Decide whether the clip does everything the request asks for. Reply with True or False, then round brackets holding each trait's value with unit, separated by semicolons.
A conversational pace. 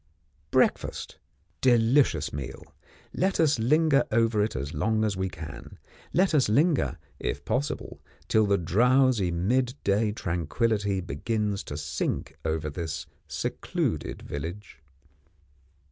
False (115 wpm)